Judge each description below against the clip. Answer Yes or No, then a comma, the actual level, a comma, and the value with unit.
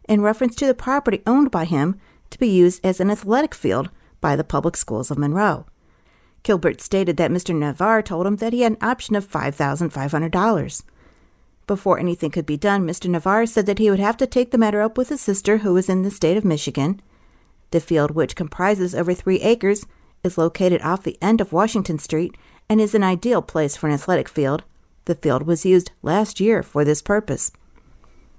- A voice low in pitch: No, medium, 185 Hz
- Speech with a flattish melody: No, average, 4.5 semitones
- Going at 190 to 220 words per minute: Yes, average, 200 wpm